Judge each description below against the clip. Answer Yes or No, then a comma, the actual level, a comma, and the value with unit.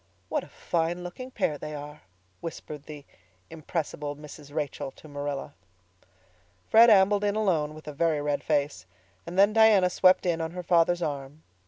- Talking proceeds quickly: No, average, 165 wpm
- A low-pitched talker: No, medium, 160 Hz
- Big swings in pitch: No, average, 3.7 semitones